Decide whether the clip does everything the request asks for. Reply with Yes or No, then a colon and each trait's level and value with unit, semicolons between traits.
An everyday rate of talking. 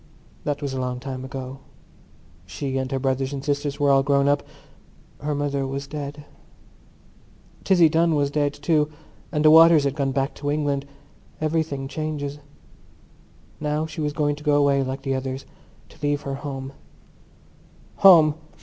Yes: average, 160 wpm